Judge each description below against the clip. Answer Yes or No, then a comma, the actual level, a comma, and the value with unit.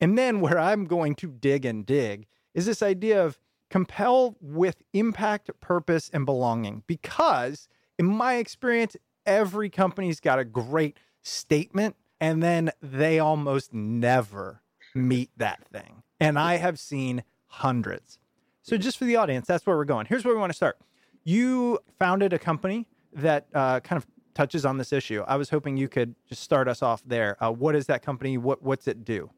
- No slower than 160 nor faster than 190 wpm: Yes, average, 180 wpm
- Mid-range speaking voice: Yes, medium, 155 Hz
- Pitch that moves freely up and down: Yes, wide, 6.5 semitones